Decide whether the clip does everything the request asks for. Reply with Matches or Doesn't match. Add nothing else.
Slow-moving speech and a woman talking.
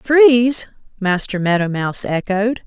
Matches